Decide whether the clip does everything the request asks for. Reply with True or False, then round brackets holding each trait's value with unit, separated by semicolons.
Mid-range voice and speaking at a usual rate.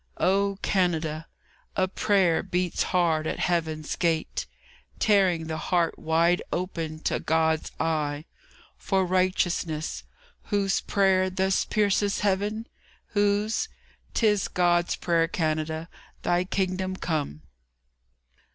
False (180 Hz; 105 wpm)